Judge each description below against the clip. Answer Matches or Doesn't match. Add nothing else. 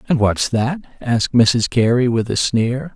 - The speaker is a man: Matches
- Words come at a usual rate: Matches